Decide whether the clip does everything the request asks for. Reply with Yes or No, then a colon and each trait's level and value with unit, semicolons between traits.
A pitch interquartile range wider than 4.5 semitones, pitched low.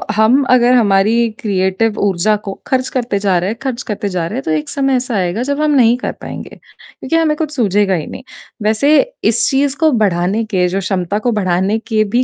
No: average, 5.0 semitones; high, 215 Hz